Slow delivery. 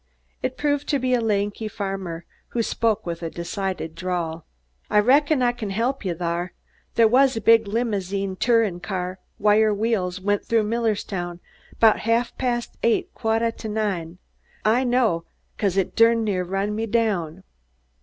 No: average, 165 wpm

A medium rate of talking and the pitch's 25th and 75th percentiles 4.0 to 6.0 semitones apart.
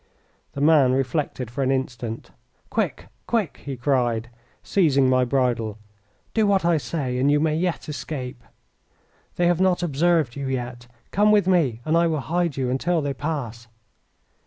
Yes: average, 160 wpm; average, 5.0 semitones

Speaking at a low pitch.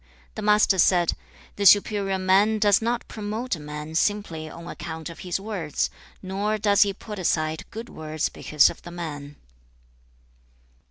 No: high, 190 Hz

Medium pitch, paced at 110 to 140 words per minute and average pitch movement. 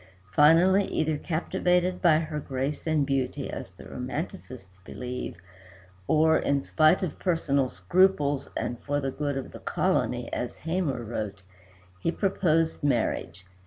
Yes: medium, 150 Hz; slow, 135 wpm; average, 4.1 semitones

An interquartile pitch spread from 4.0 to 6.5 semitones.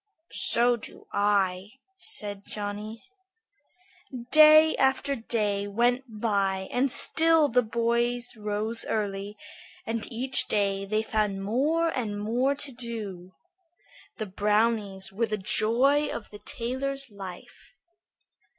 No: average, 3.5 semitones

